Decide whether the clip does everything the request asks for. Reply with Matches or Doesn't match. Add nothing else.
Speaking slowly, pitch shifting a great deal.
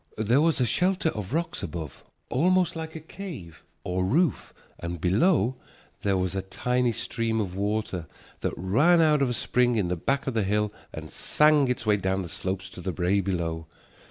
Doesn't match